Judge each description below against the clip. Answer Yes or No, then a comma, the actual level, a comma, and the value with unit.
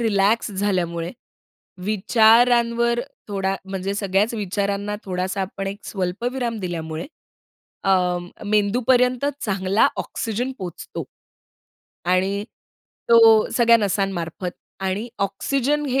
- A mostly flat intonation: No, average, 3.5 semitones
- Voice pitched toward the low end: No, high, 200 Hz